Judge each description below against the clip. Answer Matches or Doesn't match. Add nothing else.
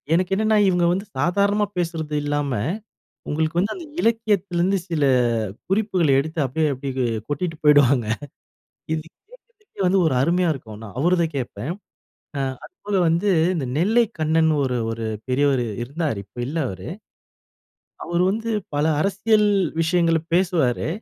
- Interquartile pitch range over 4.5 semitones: Matches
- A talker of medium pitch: Matches